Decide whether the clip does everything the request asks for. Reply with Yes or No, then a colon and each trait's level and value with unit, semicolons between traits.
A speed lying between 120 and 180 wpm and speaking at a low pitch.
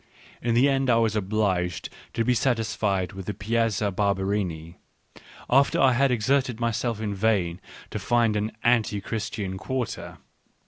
Yes: average, 145 wpm; low, 110 Hz